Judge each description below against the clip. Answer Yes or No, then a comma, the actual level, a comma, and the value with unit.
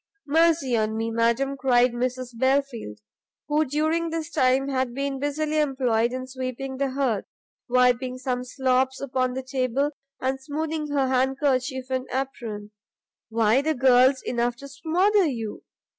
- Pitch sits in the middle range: No, very high, 260 Hz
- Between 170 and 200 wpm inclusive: No, average, 145 wpm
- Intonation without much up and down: Yes, narrow, 2.0 semitones